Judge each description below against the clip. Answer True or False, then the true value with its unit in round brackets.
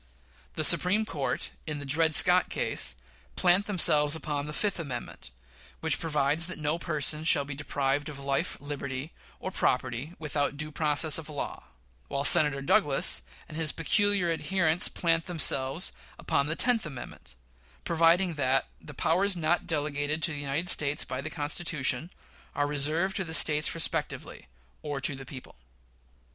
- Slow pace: False (155 wpm)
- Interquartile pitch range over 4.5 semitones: False (2.8 semitones)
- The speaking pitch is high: False (150 Hz)